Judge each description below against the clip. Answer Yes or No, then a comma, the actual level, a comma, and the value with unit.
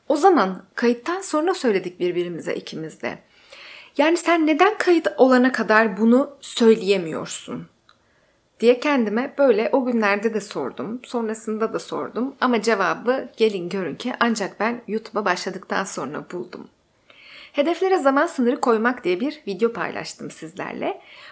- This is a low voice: No, high, 240 Hz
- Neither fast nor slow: Yes, average, 130 wpm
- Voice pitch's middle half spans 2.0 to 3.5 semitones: No, average, 4.6 semitones